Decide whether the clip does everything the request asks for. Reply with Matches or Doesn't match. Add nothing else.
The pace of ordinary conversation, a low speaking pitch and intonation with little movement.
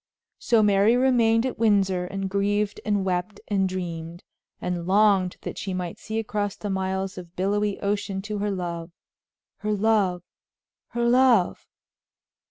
Doesn't match